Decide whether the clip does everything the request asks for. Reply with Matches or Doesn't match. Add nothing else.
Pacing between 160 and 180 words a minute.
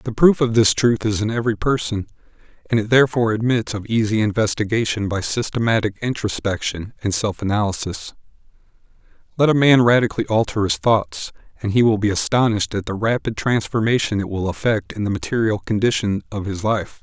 Matches